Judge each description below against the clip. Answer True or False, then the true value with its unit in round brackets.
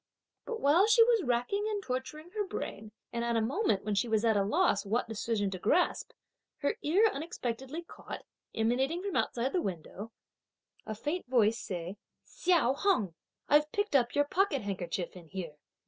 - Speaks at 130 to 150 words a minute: False (175 wpm)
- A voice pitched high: True (250 Hz)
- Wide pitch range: True (8.4 semitones)